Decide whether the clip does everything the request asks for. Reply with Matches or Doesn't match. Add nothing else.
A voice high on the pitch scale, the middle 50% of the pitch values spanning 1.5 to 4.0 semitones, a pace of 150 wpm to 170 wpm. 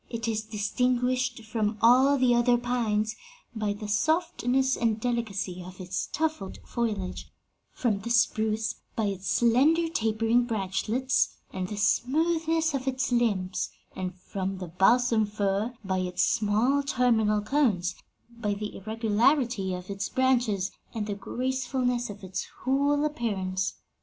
Doesn't match